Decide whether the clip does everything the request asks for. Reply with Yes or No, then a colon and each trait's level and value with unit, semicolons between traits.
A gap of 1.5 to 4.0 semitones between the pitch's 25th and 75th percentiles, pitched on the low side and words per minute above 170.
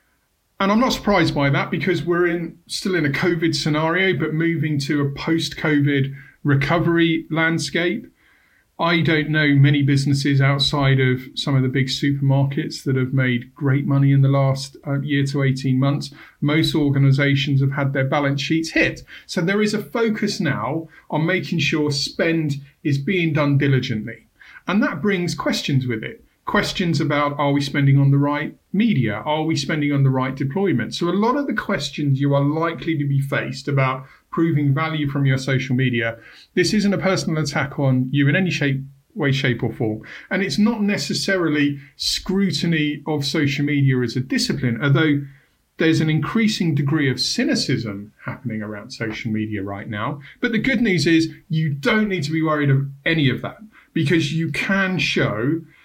No: average, 3.5 semitones; medium, 150 Hz; average, 180 wpm